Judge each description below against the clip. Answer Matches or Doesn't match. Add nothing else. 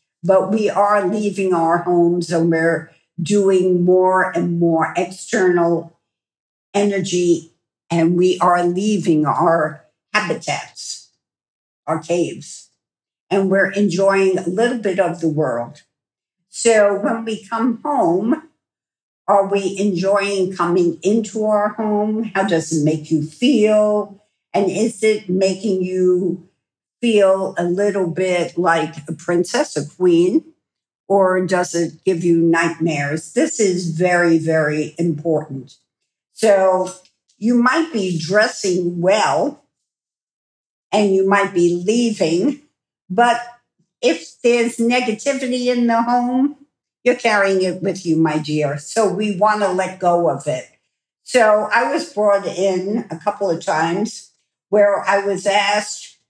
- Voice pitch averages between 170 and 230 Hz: Matches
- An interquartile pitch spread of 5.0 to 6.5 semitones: Doesn't match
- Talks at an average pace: Doesn't match